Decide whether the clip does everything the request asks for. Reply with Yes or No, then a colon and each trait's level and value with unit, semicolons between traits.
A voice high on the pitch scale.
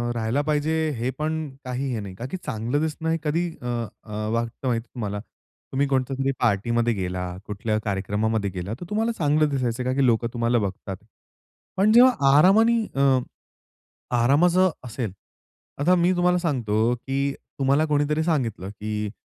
No: low, 130 Hz